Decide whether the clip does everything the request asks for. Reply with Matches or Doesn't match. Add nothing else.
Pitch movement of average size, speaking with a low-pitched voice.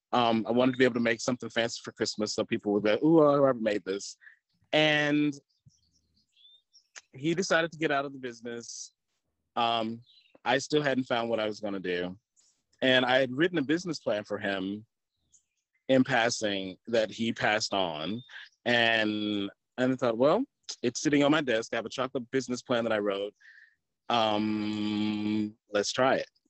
Matches